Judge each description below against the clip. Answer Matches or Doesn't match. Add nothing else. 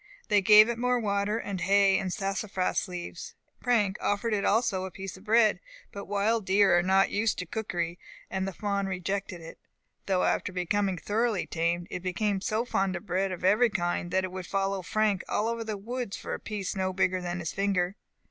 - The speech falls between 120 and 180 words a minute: Doesn't match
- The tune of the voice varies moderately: Doesn't match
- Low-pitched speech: Doesn't match